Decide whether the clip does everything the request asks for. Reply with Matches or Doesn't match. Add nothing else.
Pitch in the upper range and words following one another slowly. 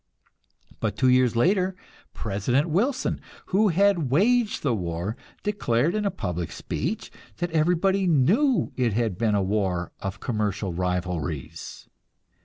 Doesn't match